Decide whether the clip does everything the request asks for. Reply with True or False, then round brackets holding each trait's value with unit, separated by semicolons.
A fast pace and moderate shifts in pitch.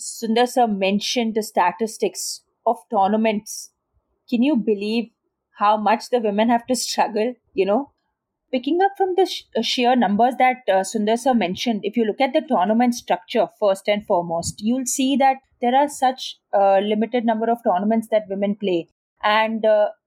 False (175 wpm; 3.1 semitones)